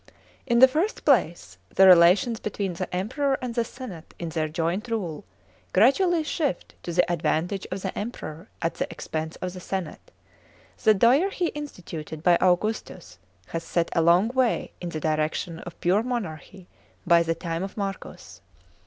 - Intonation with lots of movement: Yes, wide, 5.8 semitones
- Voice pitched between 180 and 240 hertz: Yes, medium, 185 Hz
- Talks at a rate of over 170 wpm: No, average, 165 wpm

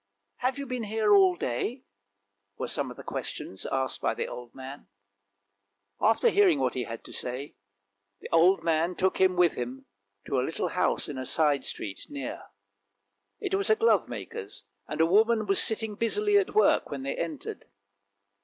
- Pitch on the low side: No, medium, 185 Hz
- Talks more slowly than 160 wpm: No, average, 180 wpm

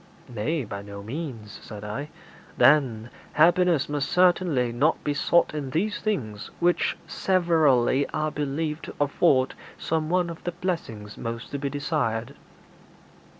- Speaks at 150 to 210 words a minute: No, average, 140 wpm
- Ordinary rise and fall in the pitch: No, wide, 5.7 semitones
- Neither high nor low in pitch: Yes, medium, 145 Hz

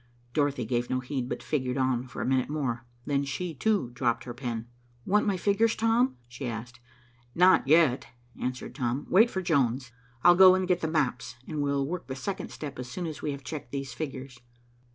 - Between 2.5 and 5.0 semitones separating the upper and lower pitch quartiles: No, wide, 5.4 semitones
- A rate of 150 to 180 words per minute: No, average, 200 wpm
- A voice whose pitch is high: No, medium, 140 Hz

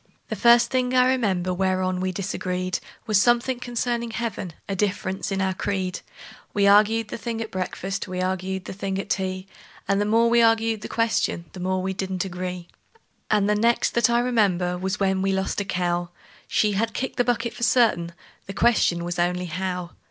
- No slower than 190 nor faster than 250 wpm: Yes, average, 195 wpm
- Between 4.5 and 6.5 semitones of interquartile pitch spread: No, average, 3.6 semitones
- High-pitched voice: Yes, high, 195 Hz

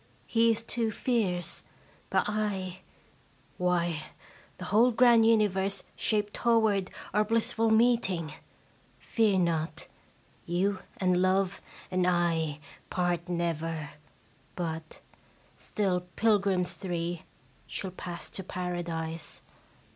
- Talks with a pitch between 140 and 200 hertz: Yes, medium, 185 Hz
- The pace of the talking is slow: Yes, slow, 100 wpm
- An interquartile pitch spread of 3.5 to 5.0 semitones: Yes, average, 3.8 semitones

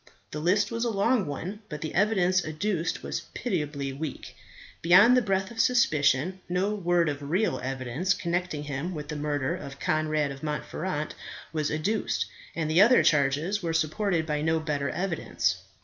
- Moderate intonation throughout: Yes, average, 4.4 semitones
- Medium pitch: Yes, medium, 160 Hz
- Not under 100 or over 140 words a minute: No, average, 165 wpm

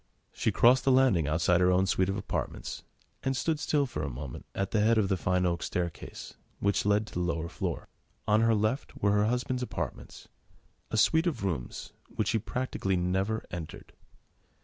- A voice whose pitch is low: Yes, low, 100 Hz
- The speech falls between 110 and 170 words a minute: No, average, 190 wpm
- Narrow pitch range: No, average, 4.8 semitones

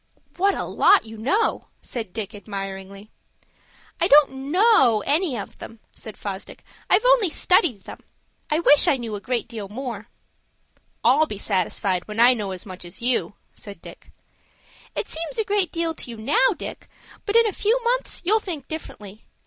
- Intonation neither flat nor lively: No, wide, 8.6 semitones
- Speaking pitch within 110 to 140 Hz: No, high, 245 Hz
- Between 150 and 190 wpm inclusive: Yes, average, 175 wpm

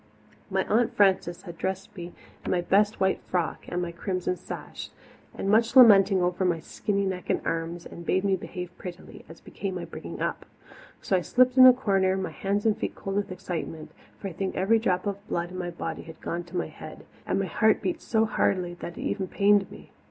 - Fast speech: Yes, fast, 220 wpm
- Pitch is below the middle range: No, high, 190 Hz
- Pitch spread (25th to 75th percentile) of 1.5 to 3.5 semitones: Yes, narrow, 2.4 semitones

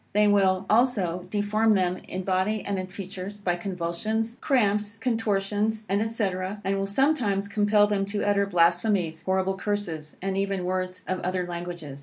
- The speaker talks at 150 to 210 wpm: Yes, average, 155 wpm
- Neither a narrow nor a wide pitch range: No, narrow, 2.3 semitones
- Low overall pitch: No, high, 195 Hz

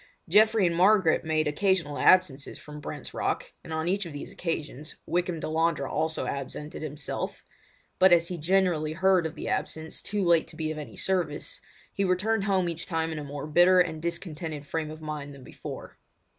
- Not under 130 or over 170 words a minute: No, average, 185 wpm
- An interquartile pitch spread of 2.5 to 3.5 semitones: Yes, average, 3.1 semitones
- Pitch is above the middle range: No, medium, 160 Hz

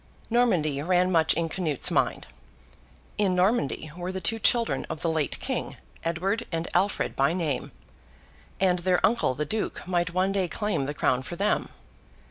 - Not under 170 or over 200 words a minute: No, average, 160 wpm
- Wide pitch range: No, average, 3.4 semitones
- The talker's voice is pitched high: No, medium, 180 Hz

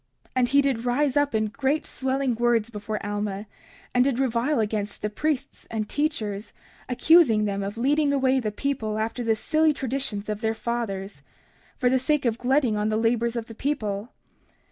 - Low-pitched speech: No, high, 235 Hz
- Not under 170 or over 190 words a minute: Yes, average, 185 wpm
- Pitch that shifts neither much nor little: Yes, average, 4.1 semitones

